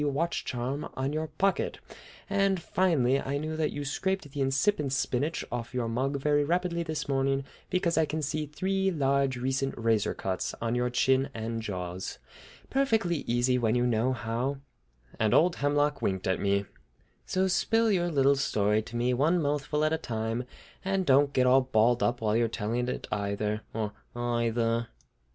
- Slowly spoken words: No, average, 175 wpm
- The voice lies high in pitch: No, low, 135 Hz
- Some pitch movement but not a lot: Yes, average, 4.9 semitones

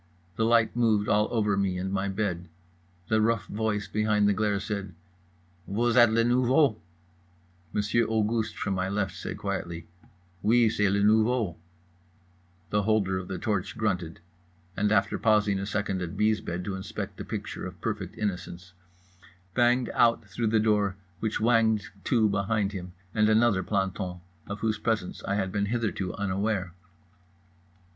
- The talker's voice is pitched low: Yes, low, 105 Hz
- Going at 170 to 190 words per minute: No, average, 155 wpm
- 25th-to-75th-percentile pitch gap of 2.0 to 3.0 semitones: Yes, narrow, 2.4 semitones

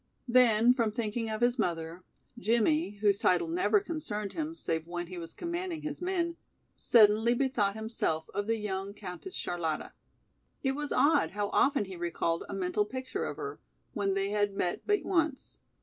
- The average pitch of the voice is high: Yes, high, 220 Hz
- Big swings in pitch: Yes, wide, 6.8 semitones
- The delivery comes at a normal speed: Yes, average, 170 wpm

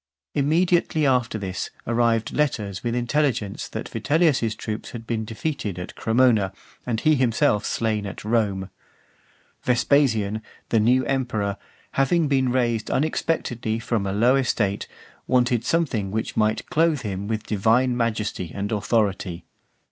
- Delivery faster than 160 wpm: No, slow, 135 wpm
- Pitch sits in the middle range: No, low, 115 Hz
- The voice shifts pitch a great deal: No, average, 3.6 semitones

